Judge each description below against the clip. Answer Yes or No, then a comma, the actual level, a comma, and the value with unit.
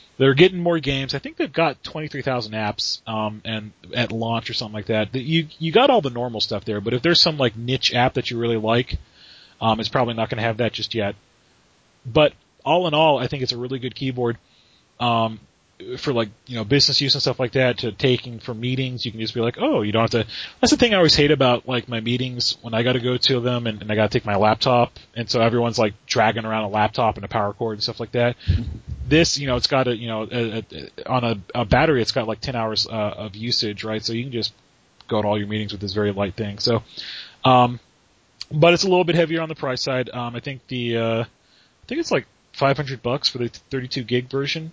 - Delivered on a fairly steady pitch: No, average, 3.1 semitones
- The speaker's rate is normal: No, fast, 260 wpm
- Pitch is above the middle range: No, low, 120 Hz